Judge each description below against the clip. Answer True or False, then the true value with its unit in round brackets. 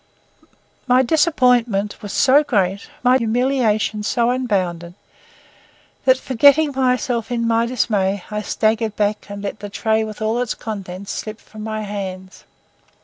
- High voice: True (220 Hz)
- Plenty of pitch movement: False (3.4 semitones)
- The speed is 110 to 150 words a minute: True (140 wpm)